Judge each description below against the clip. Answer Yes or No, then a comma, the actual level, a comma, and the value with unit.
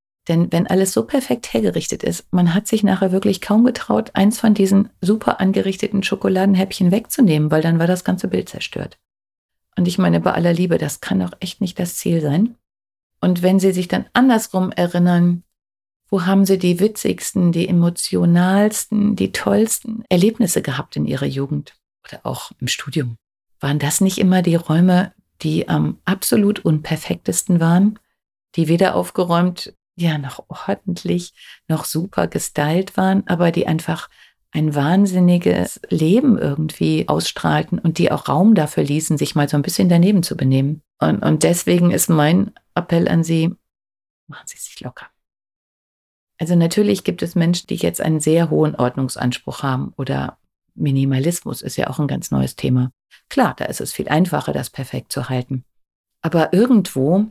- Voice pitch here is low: No, medium, 175 Hz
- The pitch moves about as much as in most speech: Yes, average, 3.8 semitones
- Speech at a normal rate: Yes, average, 160 wpm